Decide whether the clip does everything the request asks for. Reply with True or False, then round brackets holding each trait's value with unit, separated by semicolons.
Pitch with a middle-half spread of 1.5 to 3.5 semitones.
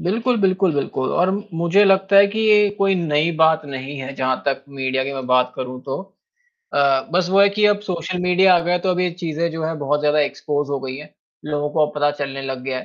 False (5.3 semitones)